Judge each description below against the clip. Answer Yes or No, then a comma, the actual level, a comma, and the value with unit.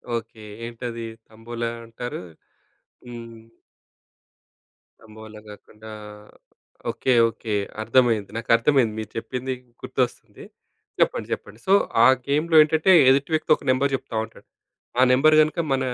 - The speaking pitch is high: No, low, 120 Hz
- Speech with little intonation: No, average, 3.2 semitones